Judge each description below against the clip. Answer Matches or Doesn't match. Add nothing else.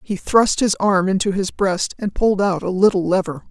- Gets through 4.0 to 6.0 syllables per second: Matches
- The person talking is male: Doesn't match